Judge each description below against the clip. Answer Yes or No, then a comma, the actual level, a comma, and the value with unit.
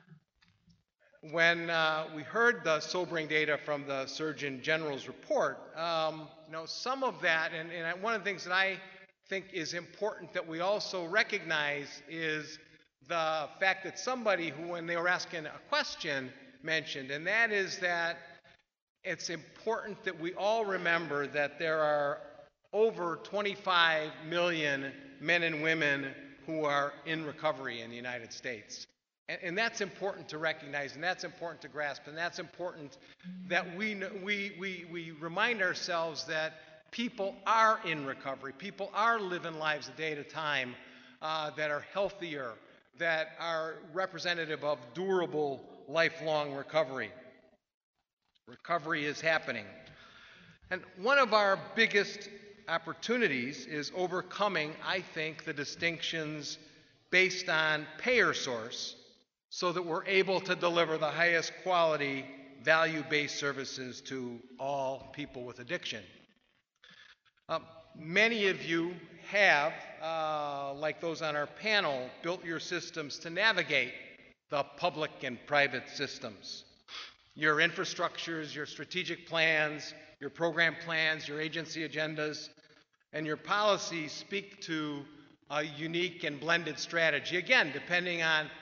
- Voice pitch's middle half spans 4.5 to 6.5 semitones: No, average, 3.1 semitones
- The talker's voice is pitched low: No, medium, 160 Hz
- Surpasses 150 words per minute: No, slow, 135 wpm